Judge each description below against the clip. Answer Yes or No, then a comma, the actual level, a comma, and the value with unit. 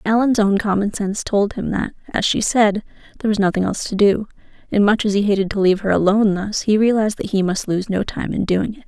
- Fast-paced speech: Yes, fast, 250 wpm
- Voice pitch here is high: Yes, high, 205 Hz